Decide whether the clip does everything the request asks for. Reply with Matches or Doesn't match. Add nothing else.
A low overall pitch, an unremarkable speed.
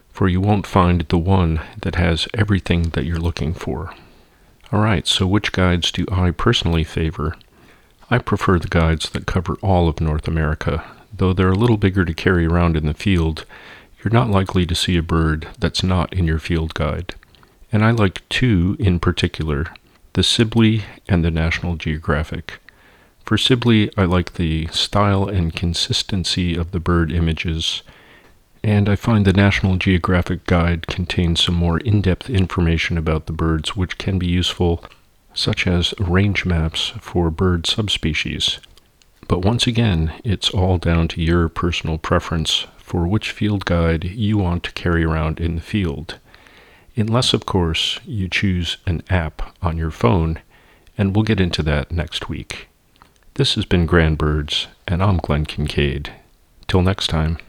Matches